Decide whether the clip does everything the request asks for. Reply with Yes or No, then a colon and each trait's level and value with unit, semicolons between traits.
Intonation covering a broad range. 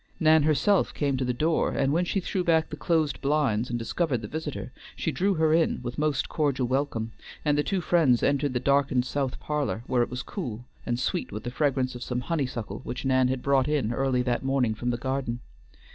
No: average, 3.7 semitones